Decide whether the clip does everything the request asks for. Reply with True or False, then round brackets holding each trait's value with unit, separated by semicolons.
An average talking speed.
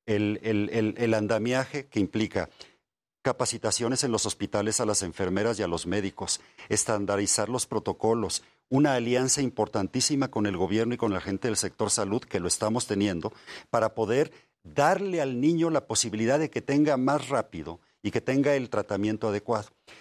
True (170 wpm)